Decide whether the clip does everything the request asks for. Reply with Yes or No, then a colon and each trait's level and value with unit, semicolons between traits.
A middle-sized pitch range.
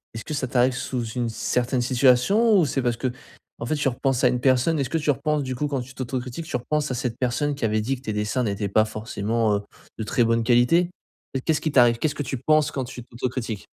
Yes: average, 3.1 semitones